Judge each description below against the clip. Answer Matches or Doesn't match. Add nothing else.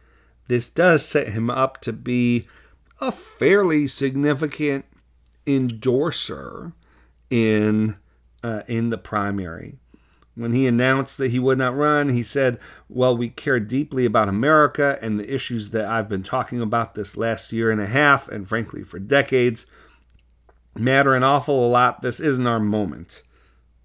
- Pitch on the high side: Doesn't match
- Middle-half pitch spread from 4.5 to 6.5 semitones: Doesn't match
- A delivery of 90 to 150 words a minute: Matches